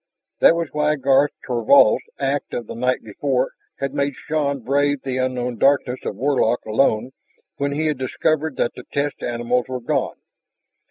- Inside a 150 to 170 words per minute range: Yes, average, 165 wpm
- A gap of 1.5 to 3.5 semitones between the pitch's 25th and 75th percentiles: Yes, narrow, 2.4 semitones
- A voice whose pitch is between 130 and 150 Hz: Yes, low, 135 Hz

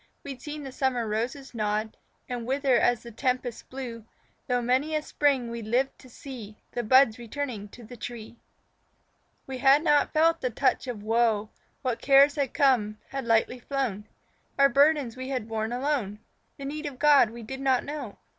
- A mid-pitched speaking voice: No, very high, 255 Hz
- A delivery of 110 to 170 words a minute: No, average, 180 wpm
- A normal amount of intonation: Yes, average, 3.2 semitones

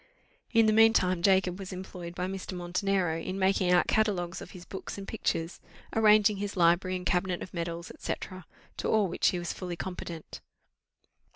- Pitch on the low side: No, medium, 185 Hz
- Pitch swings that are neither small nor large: No, narrow, 2.1 semitones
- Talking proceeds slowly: No, average, 180 wpm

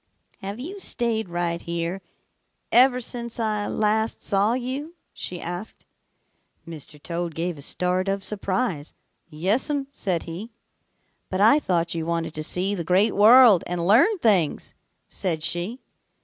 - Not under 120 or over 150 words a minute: Yes, average, 140 wpm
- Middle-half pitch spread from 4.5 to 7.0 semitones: Yes, average, 5.1 semitones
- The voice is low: No, high, 195 Hz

